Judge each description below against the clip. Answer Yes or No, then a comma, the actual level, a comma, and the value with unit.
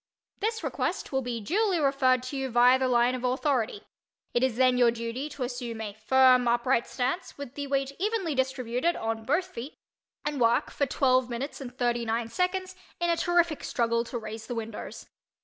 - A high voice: Yes, very high, 255 Hz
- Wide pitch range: No, average, 3.1 semitones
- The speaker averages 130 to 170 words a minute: No, average, 190 wpm